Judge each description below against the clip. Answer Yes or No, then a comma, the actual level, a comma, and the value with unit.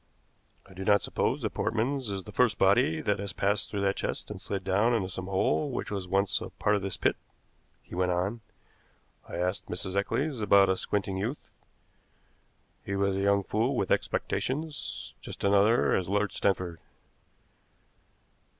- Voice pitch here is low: Yes, low, 100 Hz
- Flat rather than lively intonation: Yes, narrow, 1.9 semitones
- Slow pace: No, average, 175 wpm